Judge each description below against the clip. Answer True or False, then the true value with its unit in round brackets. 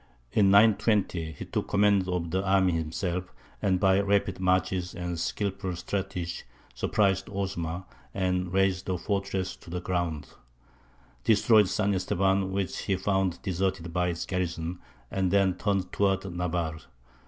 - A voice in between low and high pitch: False (95 Hz)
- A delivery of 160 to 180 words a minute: False (140 wpm)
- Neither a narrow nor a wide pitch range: False (1.8 semitones)